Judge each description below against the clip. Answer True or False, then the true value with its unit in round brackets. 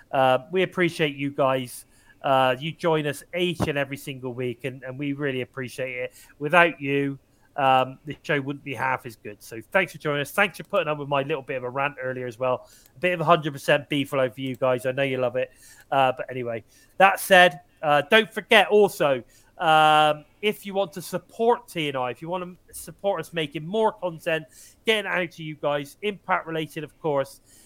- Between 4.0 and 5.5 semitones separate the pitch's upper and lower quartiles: True (5.0 semitones)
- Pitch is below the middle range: False (145 Hz)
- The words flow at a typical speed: False (210 wpm)